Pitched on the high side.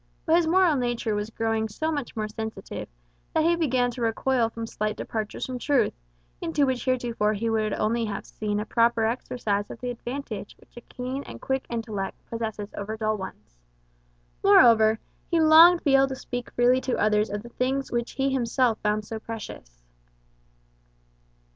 Yes: high, 230 Hz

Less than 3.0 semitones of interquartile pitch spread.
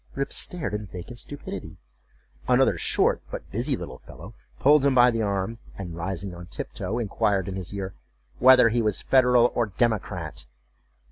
No: average, 4.4 semitones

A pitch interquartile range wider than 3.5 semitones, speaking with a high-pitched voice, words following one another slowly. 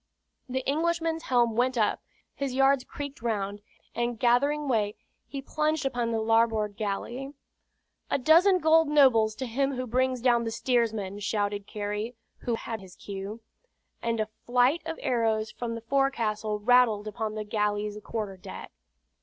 No: average, 4.0 semitones; high, 235 Hz; average, 155 wpm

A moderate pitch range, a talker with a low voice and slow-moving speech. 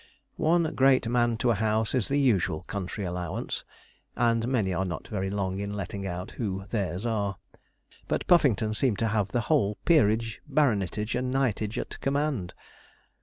No: average, 4.2 semitones; low, 110 Hz; average, 165 wpm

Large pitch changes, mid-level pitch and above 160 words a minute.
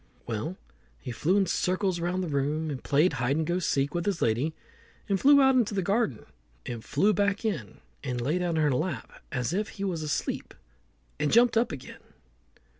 Yes: wide, 6.0 semitones; medium, 170 Hz; average, 195 wpm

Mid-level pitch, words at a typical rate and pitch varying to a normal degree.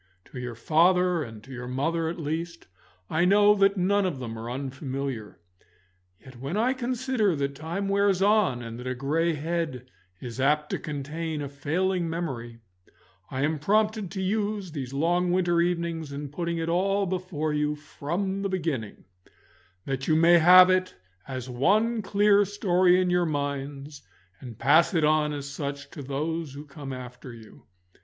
Yes: medium, 160 Hz; average, 170 wpm; average, 5.0 semitones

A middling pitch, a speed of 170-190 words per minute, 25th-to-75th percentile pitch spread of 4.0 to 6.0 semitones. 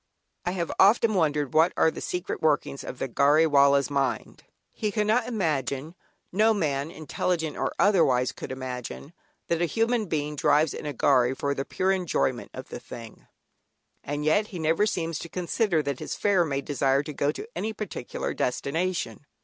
Yes: medium, 155 Hz; average, 175 wpm; average, 4.9 semitones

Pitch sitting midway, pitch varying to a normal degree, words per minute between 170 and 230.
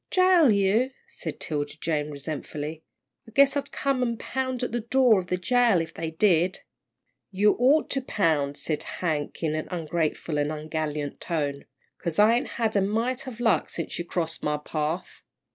No: medium, 180 Hz; wide, 7.6 semitones; average, 180 wpm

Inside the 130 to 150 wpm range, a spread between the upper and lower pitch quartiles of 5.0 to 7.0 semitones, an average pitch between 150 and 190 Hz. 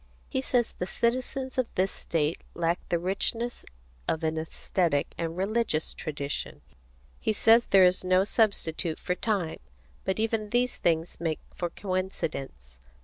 Yes: average, 145 wpm; wide, 5.5 semitones; medium, 185 Hz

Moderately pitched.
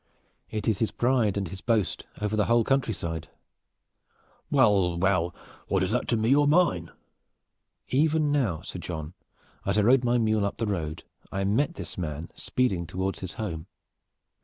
No: low, 100 Hz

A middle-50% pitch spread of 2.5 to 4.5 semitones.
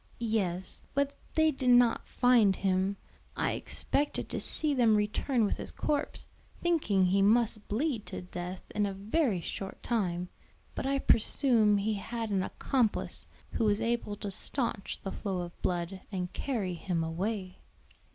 Yes: average, 4.2 semitones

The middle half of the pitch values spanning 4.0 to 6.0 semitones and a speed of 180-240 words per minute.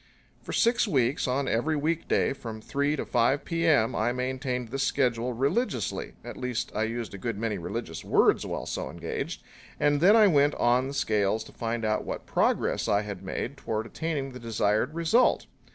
Yes: average, 4.4 semitones; average, 185 wpm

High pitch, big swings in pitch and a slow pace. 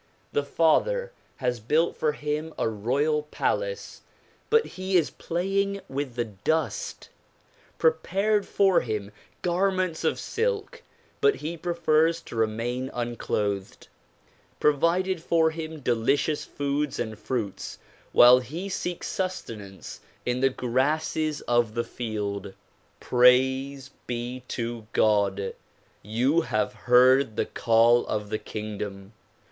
No: low, 135 Hz; wide, 6.3 semitones; slow, 115 wpm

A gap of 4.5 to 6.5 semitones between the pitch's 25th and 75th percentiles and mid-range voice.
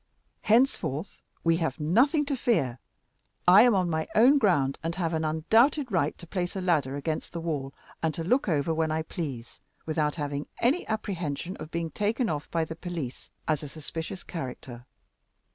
Yes: average, 4.9 semitones; medium, 165 Hz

